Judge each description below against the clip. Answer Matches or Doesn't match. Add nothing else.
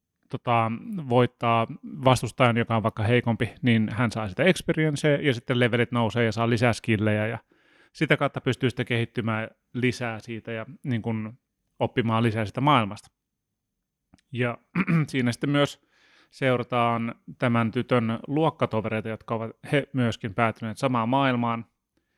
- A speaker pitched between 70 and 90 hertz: Doesn't match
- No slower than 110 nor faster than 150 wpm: Matches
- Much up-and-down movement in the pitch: Doesn't match